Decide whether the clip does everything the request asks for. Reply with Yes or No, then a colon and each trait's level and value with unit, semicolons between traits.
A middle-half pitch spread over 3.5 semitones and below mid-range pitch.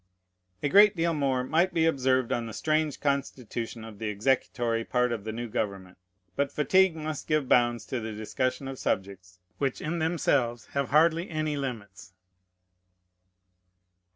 Yes: average, 5.2 semitones; low, 130 Hz